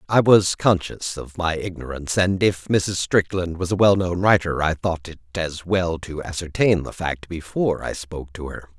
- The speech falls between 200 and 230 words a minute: No, average, 190 wpm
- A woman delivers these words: No, male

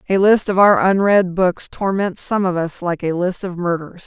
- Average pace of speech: No, fast, 220 wpm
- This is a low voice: No, medium, 185 Hz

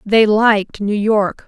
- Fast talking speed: No, average, 165 wpm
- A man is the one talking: No, female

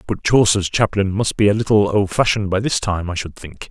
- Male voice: Yes, male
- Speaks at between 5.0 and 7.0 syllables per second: Yes, 5.6 syllables/s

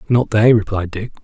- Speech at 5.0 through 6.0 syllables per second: Yes, 5.2 syllables/s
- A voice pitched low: Yes, low, 110 Hz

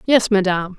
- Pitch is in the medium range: No, high, 200 Hz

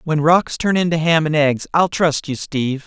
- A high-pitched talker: No, medium, 155 Hz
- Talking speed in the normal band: No, fast, 230 wpm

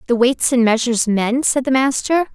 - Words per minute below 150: No, fast, 205 wpm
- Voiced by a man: No, female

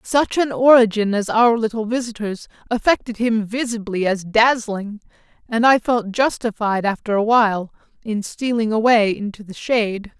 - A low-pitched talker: No, high, 220 Hz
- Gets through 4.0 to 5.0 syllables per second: Yes, 4.7 syllables/s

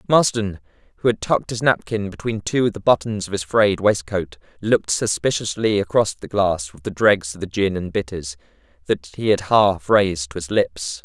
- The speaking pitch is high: No, low, 100 Hz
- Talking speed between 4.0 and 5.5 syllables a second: Yes, 5.1 syllables/s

